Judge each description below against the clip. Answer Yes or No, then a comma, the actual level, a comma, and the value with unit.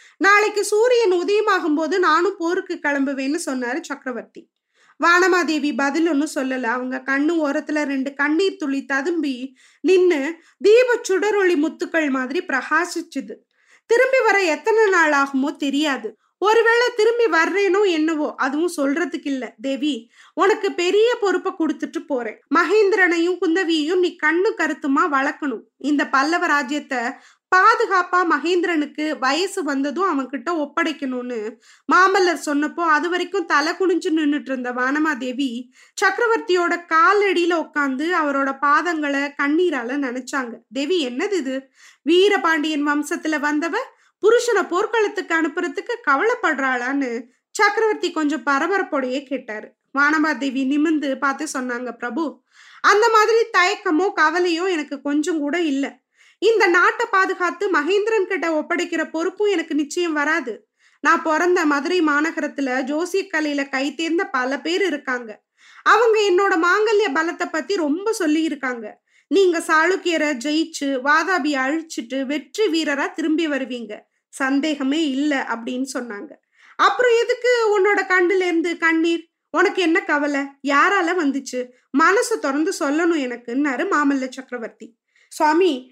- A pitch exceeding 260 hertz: Yes, very high, 315 Hz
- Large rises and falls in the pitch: No, average, 4.8 semitones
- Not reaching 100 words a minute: No, average, 110 wpm